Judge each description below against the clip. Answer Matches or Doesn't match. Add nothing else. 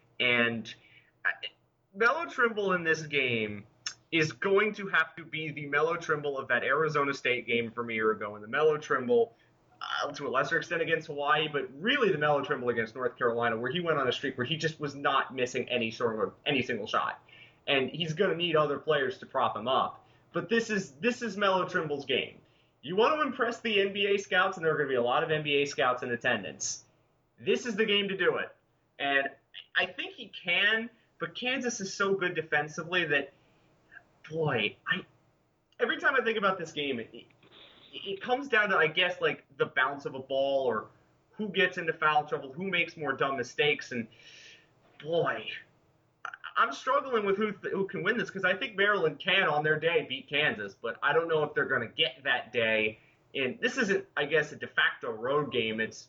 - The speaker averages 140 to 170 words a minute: Doesn't match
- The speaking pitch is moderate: Matches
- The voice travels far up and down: Matches